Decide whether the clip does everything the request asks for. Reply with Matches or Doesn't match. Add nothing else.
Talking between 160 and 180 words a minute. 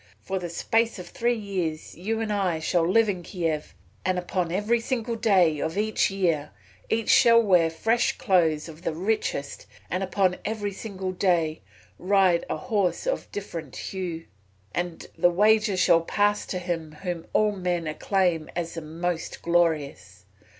Matches